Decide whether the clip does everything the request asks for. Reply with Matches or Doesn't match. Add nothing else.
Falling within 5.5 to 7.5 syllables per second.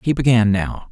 Doesn't match